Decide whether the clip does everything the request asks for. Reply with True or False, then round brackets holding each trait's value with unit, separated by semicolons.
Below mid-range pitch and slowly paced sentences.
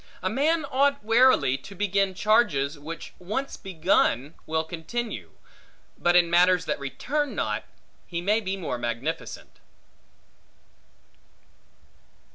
False (185 Hz; 110 wpm)